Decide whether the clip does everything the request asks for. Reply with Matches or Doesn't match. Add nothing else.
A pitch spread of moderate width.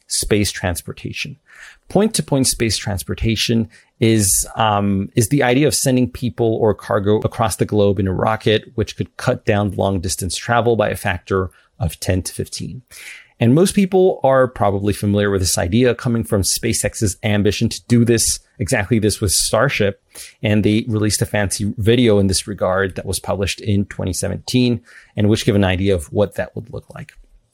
Matches